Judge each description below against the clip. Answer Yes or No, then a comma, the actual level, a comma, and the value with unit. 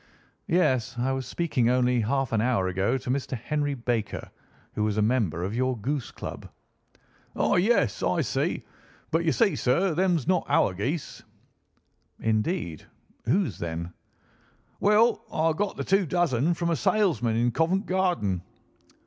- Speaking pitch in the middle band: No, low, 130 Hz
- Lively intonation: Yes, wide, 7.2 semitones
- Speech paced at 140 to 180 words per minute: Yes, average, 150 wpm